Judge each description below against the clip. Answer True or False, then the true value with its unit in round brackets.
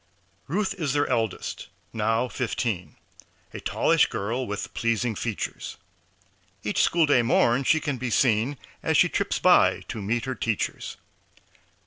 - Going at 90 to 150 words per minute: True (140 wpm)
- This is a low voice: True (120 Hz)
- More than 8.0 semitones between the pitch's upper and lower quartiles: False (3.2 semitones)